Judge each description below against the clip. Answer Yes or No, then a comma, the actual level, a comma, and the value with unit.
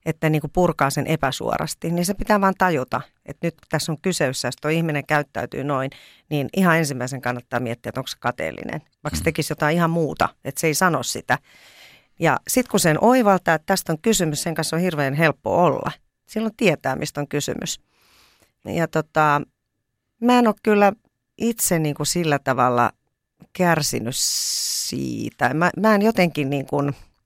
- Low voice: No, medium, 155 Hz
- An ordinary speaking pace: No, fast, 180 wpm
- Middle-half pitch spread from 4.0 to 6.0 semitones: Yes, average, 4.7 semitones